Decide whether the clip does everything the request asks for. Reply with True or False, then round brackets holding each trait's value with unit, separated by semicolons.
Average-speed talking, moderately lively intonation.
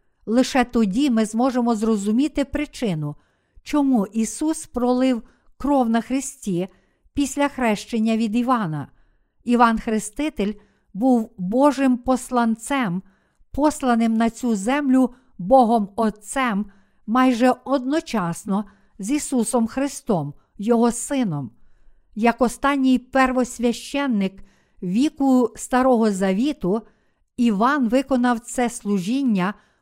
False (90 wpm; 3.2 semitones)